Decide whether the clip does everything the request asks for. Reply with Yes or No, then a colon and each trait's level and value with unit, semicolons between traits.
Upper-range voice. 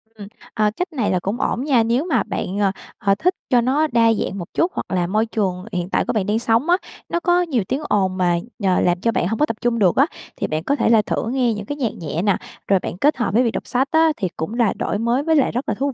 Yes: high, 230 Hz